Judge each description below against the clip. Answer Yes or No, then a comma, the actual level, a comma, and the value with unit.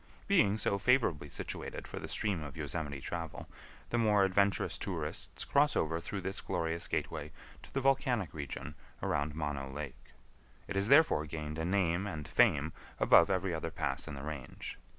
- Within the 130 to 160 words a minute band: No, average, 170 wpm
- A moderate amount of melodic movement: Yes, average, 5.0 semitones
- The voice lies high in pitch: No, very low, 85 Hz